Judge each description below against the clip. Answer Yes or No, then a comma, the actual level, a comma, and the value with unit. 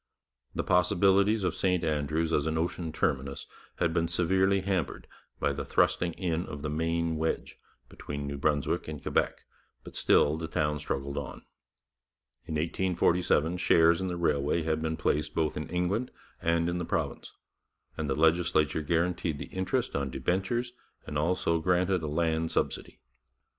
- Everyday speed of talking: Yes, average, 160 wpm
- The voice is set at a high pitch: No, very low, 80 Hz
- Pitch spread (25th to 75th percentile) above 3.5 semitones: No, average, 2.7 semitones